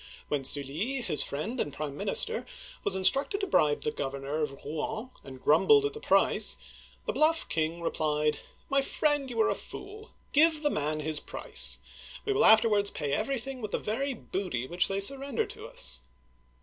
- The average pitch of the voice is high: Yes, high, 200 Hz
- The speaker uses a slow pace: No, average, 185 wpm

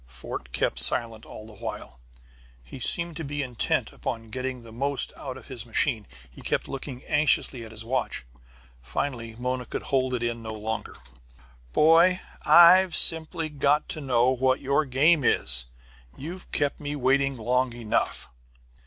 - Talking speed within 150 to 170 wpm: Yes, average, 155 wpm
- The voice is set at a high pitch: No, low, 130 Hz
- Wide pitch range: No, average, 4.0 semitones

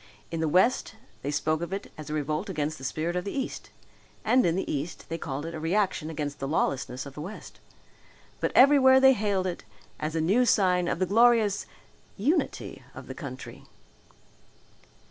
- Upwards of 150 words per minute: Yes, average, 185 wpm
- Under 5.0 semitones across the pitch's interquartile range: No, wide, 5.4 semitones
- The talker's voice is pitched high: No, medium, 175 Hz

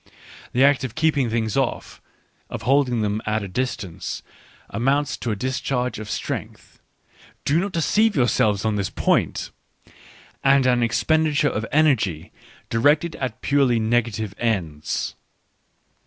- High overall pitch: No, low, 125 Hz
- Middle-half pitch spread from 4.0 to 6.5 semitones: Yes, average, 4.5 semitones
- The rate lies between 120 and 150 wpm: Yes, average, 140 wpm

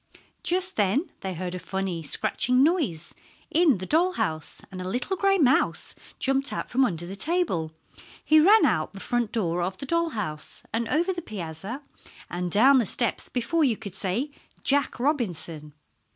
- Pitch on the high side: Yes, high, 235 Hz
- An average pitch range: No, wide, 8.8 semitones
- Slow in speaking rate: No, average, 175 wpm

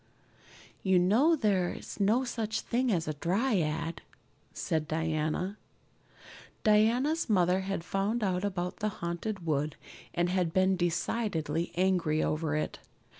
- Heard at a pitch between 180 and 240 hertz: Yes, medium, 185 Hz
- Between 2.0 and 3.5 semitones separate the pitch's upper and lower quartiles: No, average, 4.4 semitones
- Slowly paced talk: Yes, slow, 125 wpm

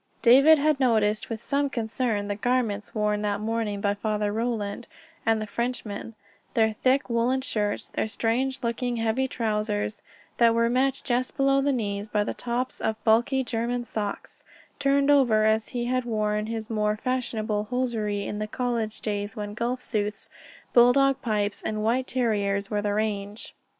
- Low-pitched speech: No, high, 225 Hz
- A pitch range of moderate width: Yes, average, 3.0 semitones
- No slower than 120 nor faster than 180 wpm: Yes, average, 165 wpm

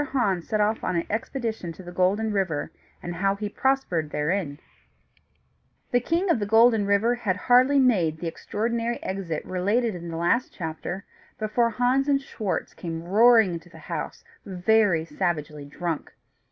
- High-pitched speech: Yes, high, 200 Hz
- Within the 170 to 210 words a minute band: No, average, 160 wpm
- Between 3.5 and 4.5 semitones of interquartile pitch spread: No, average, 5.2 semitones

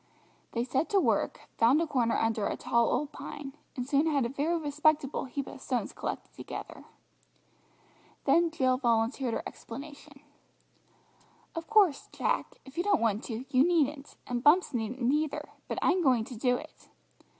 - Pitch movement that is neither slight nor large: Yes, average, 4.0 semitones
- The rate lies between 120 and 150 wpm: No, average, 165 wpm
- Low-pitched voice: No, very high, 275 Hz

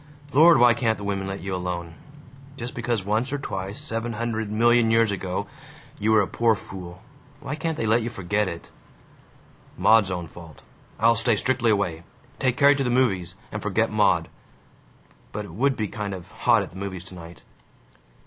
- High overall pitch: No, low, 110 Hz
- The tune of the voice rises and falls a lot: No, average, 3.9 semitones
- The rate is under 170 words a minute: No, average, 185 wpm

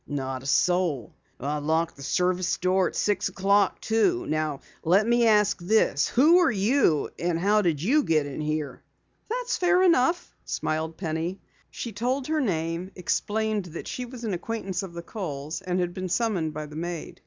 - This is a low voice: No, medium, 185 Hz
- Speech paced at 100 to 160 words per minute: No, average, 180 wpm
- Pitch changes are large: Yes, wide, 5.8 semitones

